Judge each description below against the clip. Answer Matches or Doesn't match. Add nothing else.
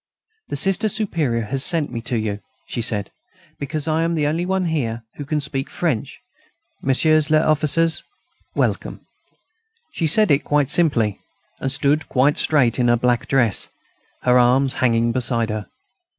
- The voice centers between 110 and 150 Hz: Matches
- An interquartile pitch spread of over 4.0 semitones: Matches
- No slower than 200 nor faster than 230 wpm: Doesn't match